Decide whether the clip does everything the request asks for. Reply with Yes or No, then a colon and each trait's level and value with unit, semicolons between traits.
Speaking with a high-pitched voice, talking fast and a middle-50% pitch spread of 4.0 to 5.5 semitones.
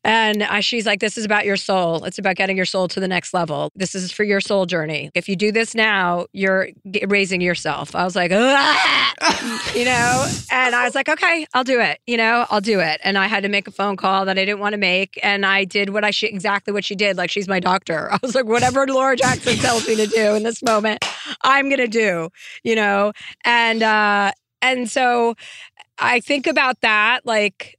No: high, 210 Hz; fast, 225 wpm; average, 3.6 semitones